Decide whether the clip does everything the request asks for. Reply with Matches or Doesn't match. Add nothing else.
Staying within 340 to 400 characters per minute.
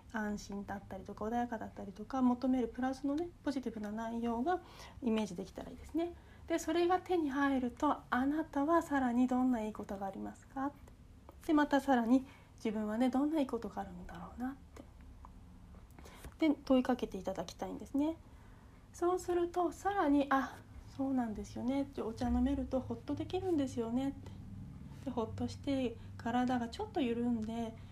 Matches